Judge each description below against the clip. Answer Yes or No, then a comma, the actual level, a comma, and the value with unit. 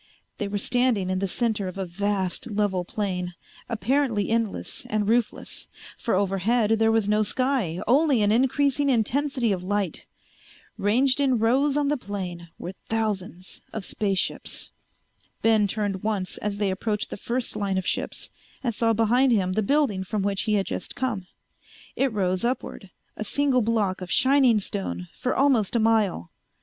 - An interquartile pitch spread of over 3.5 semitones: Yes, average, 3.9 semitones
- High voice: Yes, high, 215 Hz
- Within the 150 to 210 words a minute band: Yes, average, 165 wpm